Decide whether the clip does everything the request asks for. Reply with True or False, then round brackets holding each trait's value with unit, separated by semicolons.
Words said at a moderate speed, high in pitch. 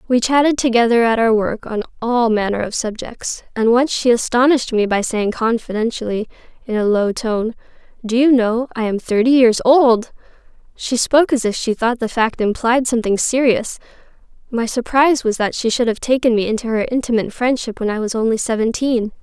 True (185 wpm; 230 Hz)